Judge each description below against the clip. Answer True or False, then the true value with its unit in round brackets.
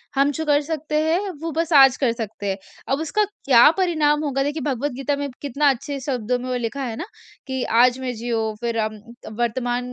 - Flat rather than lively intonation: False (3.6 semitones)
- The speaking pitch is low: False (270 Hz)